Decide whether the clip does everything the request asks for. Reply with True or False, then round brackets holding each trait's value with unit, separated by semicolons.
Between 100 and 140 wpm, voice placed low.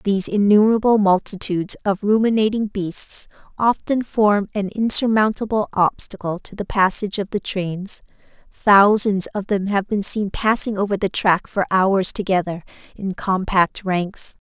False (135 wpm; 200 Hz)